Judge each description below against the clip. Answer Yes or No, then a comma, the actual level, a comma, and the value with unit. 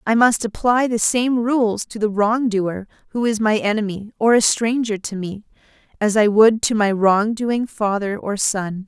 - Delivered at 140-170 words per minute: No, average, 195 wpm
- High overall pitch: Yes, high, 215 Hz